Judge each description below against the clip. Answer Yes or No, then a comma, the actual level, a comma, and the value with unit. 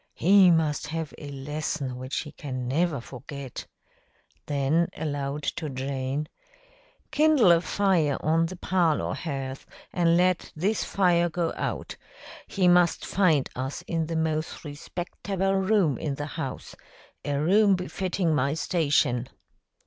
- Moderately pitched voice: Yes, medium, 160 Hz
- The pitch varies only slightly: No, average, 4.0 semitones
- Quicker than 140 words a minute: No, slow, 135 wpm